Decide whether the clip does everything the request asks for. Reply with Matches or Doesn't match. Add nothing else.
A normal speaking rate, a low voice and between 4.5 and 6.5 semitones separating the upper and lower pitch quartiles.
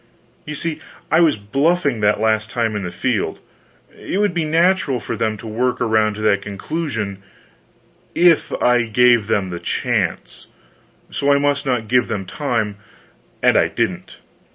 Matches